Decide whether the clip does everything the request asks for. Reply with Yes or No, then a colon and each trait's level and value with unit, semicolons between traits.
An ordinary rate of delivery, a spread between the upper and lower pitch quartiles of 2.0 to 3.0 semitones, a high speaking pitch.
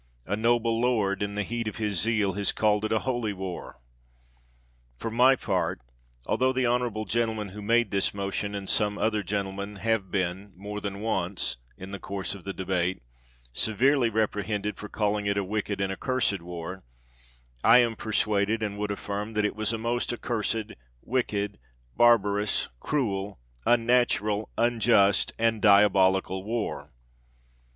No: average, 155 wpm; narrow, 2.4 semitones; low, 105 Hz